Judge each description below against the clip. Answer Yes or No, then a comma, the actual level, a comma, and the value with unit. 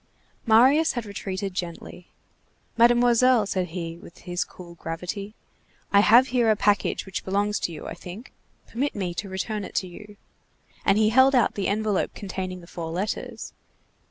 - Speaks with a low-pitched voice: No, high, 200 Hz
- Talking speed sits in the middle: Yes, average, 165 wpm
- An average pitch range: Yes, average, 3.8 semitones